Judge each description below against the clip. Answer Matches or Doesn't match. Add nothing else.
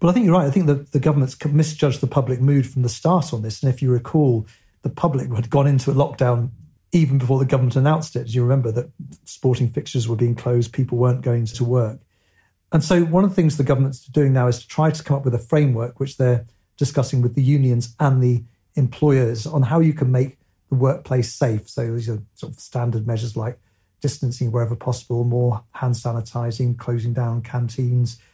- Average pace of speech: Doesn't match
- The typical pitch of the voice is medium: Doesn't match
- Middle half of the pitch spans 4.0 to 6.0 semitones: Doesn't match